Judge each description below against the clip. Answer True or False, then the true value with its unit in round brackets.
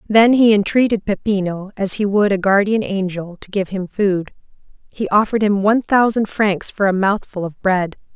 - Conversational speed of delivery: True (185 wpm)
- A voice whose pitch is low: False (200 Hz)